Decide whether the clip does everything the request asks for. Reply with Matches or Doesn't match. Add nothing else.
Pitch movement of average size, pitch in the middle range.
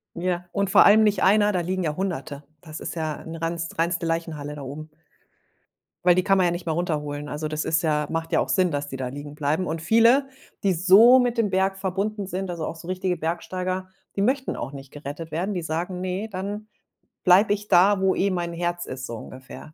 Matches